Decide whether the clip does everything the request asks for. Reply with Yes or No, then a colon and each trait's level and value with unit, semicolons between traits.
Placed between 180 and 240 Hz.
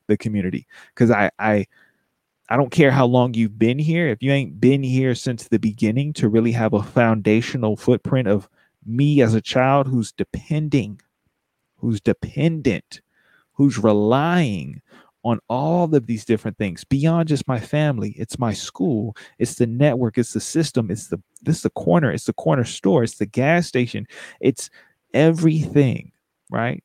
No: low, 125 Hz